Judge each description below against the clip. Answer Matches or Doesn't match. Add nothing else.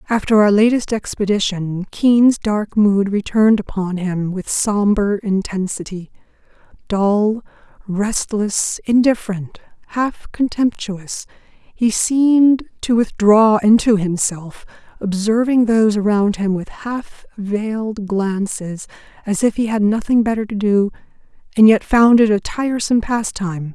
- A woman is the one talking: Matches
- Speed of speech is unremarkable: Doesn't match